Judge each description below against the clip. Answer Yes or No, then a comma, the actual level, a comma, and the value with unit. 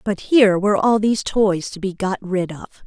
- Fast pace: Yes, fast, 230 wpm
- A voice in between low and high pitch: No, high, 200 Hz